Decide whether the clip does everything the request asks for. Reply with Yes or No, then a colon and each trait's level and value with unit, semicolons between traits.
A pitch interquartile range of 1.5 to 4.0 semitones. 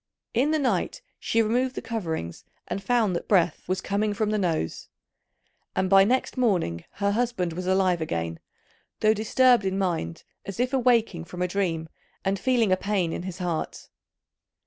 No: average, 4.6 semitones